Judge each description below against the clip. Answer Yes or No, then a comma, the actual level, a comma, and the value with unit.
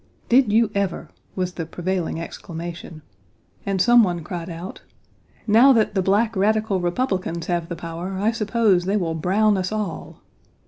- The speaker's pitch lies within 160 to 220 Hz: Yes, high, 190 Hz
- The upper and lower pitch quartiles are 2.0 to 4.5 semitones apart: Yes, average, 3.7 semitones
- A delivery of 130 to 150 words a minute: No, average, 165 wpm